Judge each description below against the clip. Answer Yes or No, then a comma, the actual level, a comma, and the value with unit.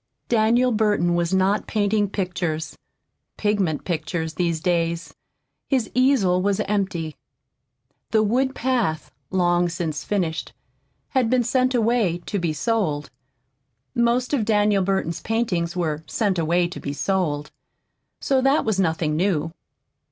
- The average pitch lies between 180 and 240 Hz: Yes, high, 190 Hz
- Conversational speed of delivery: No, slow, 130 wpm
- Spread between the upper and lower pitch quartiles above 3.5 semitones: Yes, average, 4.9 semitones